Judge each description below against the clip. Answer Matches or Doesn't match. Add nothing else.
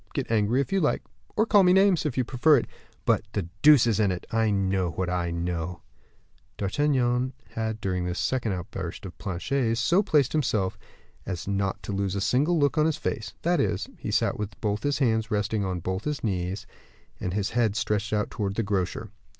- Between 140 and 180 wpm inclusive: Doesn't match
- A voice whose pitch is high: Doesn't match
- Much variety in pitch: Matches